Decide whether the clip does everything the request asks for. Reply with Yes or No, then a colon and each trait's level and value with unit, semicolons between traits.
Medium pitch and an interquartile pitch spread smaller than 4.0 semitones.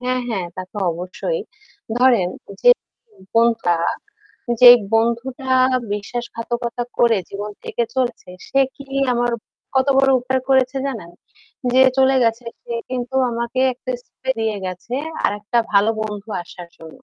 No: high, 235 Hz; average, 3.5 semitones